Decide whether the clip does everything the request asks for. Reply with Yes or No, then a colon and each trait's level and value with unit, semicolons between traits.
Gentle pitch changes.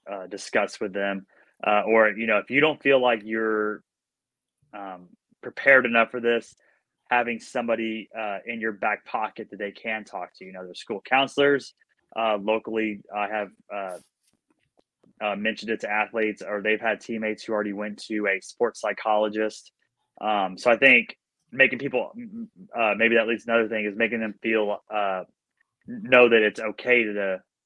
Yes: narrow, 2.1 semitones